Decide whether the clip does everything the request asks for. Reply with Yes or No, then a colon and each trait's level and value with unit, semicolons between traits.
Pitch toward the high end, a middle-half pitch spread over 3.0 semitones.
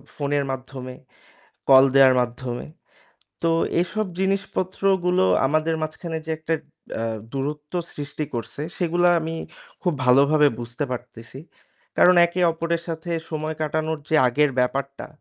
No: medium, 150 Hz; average, 3.8 semitones